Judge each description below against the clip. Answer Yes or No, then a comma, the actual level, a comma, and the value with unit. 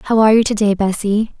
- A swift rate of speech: Yes, fast, 215 wpm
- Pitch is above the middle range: Yes, high, 210 Hz